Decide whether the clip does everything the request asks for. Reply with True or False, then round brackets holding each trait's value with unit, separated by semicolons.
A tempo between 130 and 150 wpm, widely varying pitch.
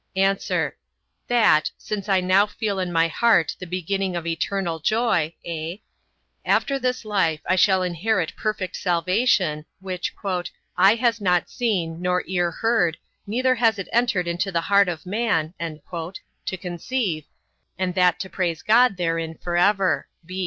False (145 wpm; 3.7 semitones)